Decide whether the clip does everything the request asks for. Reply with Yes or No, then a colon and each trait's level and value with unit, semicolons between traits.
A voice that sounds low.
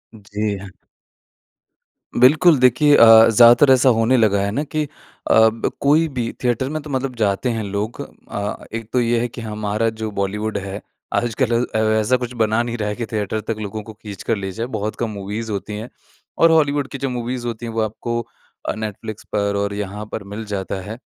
Yes: low, 115 Hz